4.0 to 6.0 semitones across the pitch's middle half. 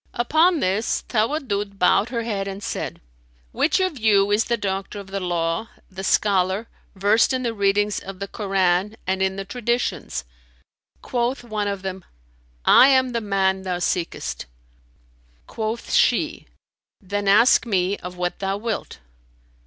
No: average, 3.3 semitones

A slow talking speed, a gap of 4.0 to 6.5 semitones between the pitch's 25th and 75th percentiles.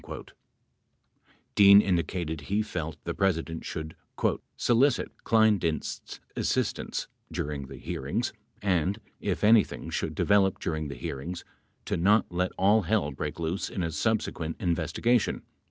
Yes: slow, 125 wpm; average, 4.3 semitones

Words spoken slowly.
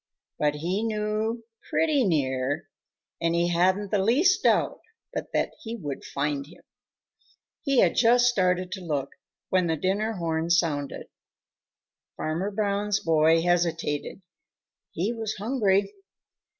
Yes: slow, 125 wpm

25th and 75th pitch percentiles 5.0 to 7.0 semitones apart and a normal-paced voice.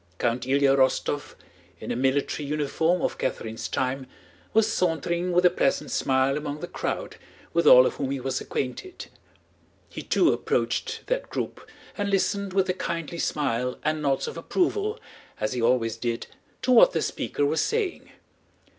Yes: wide, 5.5 semitones; average, 165 wpm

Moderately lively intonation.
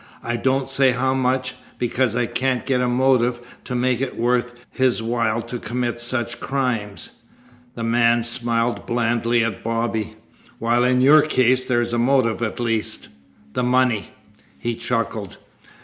No: narrow, 1.6 semitones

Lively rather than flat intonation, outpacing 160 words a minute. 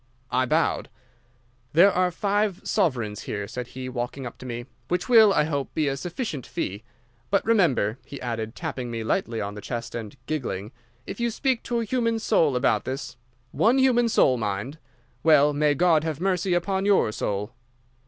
Yes: wide, 8.3 semitones; average, 175 wpm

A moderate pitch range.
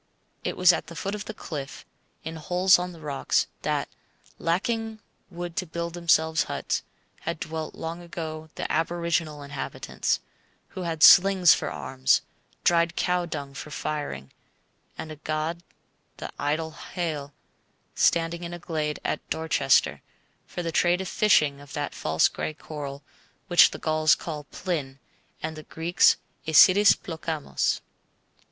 No: narrow, 2.3 semitones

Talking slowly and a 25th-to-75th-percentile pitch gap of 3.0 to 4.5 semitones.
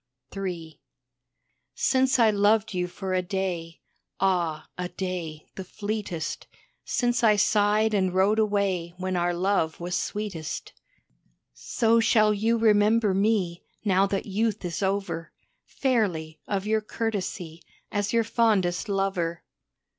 Yes: slow, 125 wpm; average, 3.3 semitones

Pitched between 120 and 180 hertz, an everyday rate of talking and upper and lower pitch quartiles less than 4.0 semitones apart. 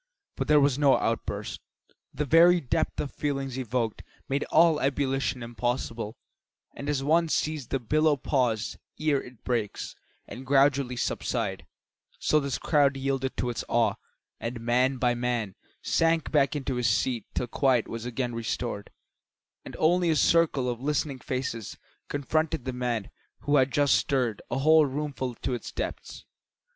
Yes: low, 135 Hz; average, 155 wpm; average, 3.1 semitones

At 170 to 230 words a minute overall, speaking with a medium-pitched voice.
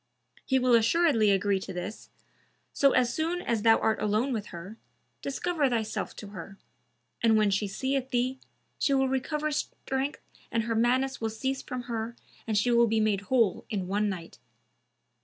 No: average, 175 wpm; high, 230 Hz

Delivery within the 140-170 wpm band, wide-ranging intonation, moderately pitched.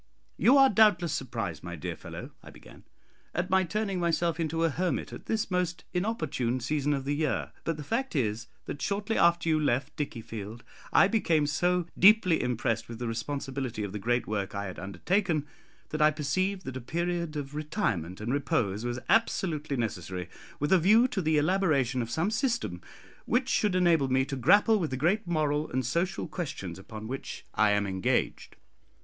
No: average, 185 wpm; wide, 7.0 semitones; medium, 150 Hz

